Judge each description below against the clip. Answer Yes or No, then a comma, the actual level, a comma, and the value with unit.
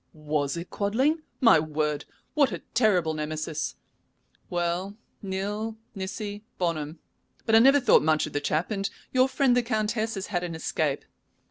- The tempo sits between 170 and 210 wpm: No, average, 155 wpm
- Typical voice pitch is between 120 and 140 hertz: No, high, 190 Hz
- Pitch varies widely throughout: Yes, wide, 6.0 semitones